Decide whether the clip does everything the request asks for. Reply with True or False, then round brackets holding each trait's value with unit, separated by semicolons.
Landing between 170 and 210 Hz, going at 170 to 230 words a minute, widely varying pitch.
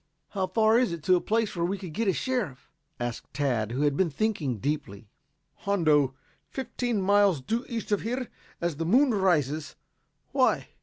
True (185 Hz; 175 wpm; 7.1 semitones)